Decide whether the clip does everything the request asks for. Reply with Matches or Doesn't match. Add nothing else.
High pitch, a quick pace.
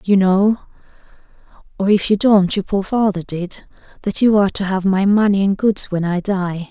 Doesn't match